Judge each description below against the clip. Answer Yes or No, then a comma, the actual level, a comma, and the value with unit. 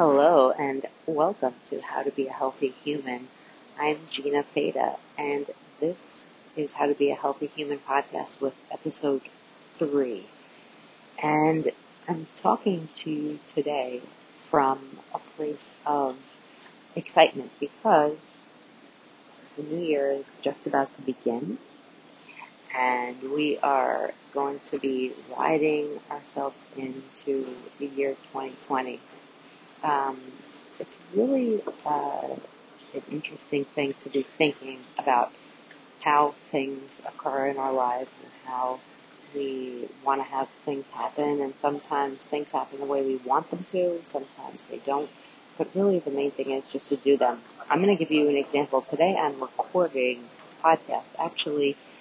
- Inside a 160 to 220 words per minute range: No, slow, 135 wpm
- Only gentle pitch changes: Yes, narrow, 1.8 semitones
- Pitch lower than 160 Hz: Yes, medium, 140 Hz